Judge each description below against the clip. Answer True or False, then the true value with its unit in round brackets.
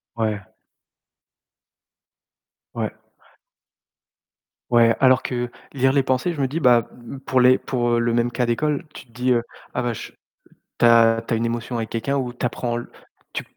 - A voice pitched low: True (120 Hz)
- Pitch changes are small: True (1.7 semitones)